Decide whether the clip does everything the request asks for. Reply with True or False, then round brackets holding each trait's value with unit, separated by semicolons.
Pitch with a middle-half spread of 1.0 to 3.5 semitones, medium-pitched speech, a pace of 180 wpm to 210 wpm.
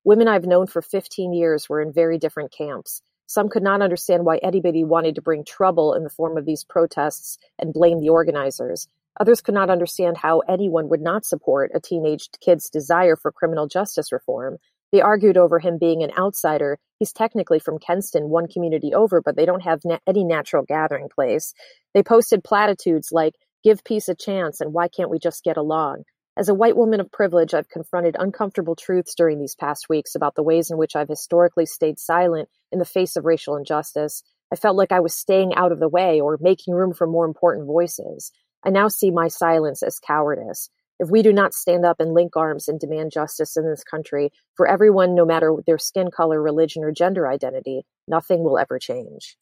True (3.0 semitones; 170 Hz; 205 wpm)